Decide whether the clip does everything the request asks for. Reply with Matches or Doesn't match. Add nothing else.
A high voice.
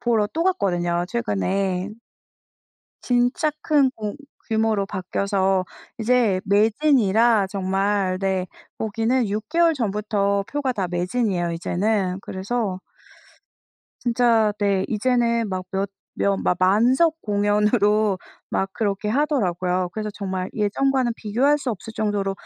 Matches